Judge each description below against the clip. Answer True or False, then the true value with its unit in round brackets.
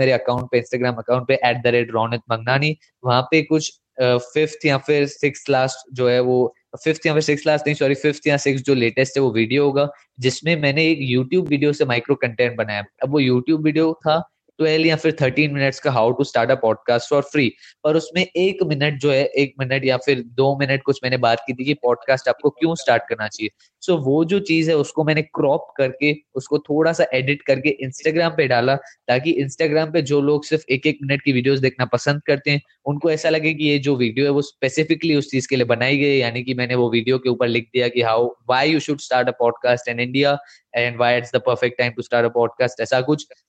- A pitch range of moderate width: True (3.3 semitones)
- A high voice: False (135 Hz)